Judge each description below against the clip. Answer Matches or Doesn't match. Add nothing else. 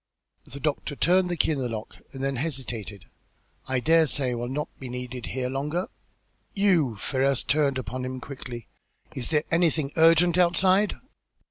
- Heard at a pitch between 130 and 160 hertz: Matches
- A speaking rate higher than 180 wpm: Doesn't match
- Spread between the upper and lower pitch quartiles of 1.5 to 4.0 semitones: Doesn't match